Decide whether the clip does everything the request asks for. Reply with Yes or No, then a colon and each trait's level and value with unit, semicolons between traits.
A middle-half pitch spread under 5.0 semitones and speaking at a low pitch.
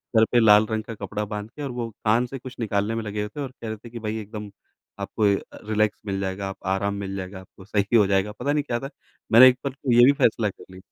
Yes: average, 2.8 semitones; low, 110 Hz